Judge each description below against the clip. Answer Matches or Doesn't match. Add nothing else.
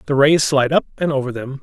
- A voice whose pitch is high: Doesn't match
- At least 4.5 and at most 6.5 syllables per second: Doesn't match